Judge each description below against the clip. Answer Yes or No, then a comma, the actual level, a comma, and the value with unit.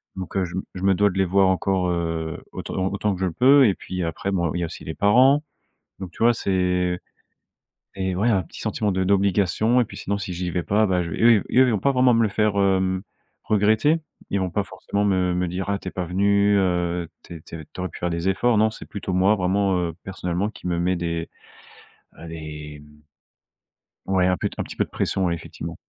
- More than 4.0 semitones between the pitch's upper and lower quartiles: No, narrow, 2.4 semitones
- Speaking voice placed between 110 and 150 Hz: No, very low, 95 Hz